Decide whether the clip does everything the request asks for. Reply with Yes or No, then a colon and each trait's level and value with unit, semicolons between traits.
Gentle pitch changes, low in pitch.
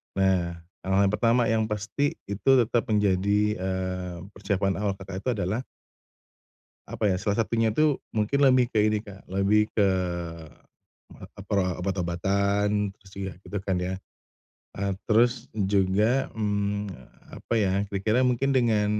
Yes: narrow, 2.3 semitones; low, 100 Hz